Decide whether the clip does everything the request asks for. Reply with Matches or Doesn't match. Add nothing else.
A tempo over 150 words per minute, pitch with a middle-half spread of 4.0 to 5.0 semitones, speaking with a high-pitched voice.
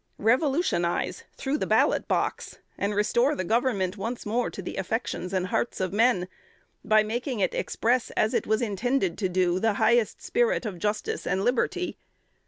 Matches